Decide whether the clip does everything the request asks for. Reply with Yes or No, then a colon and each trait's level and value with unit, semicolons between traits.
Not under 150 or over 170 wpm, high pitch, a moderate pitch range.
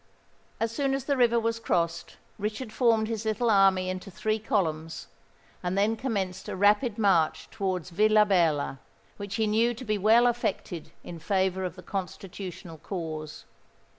Yes: average, 155 wpm; high, 200 Hz; average, 3.7 semitones